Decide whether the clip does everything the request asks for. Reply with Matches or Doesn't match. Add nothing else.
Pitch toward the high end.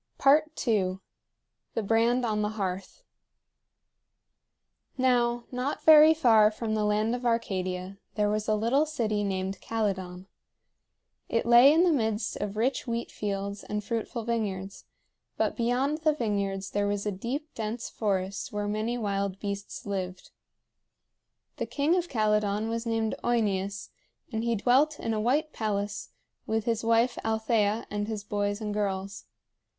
Matches